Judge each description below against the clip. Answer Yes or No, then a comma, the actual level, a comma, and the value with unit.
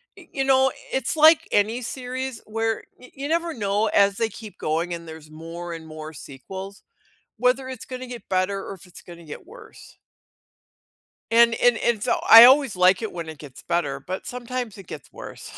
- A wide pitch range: Yes, wide, 6.5 semitones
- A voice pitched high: Yes, high, 215 Hz